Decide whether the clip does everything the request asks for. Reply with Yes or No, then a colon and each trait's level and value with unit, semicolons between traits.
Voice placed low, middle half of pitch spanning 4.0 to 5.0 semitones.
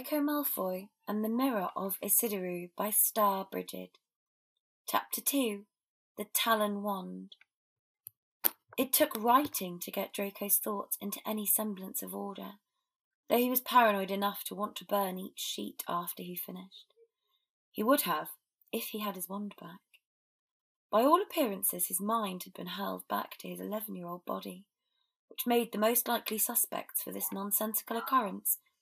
No: high, 210 Hz; average, 4.6 semitones